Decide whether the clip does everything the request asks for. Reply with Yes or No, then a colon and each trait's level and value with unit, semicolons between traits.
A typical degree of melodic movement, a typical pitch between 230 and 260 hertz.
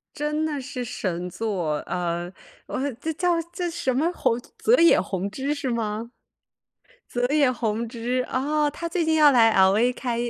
No: wide, 5.8 semitones; very high, 250 Hz